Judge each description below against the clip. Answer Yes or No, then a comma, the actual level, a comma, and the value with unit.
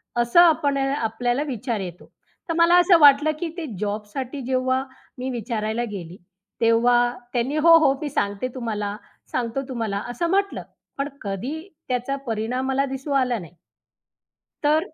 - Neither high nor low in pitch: No, very high, 255 Hz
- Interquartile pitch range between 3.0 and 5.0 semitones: Yes, average, 4.1 semitones